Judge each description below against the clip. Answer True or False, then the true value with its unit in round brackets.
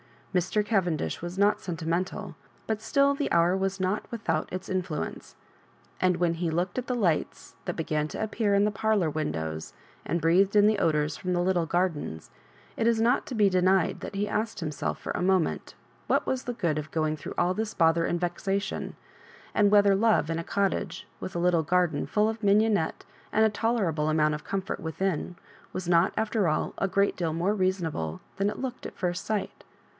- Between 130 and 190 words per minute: False (200 wpm)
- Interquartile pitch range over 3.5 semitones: True (3.9 semitones)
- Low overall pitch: False (185 Hz)